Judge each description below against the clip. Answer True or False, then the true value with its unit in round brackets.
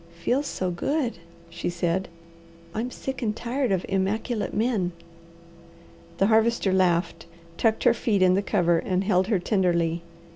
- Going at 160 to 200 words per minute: False (145 wpm)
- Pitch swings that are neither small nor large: True (4.5 semitones)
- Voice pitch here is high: True (195 Hz)